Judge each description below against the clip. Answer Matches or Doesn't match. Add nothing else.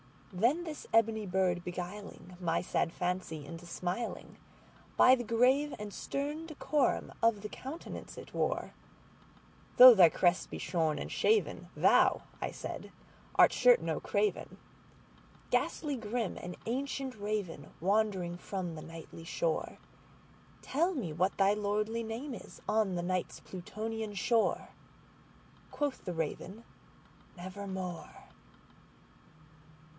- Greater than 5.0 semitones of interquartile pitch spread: Matches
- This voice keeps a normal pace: Doesn't match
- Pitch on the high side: Matches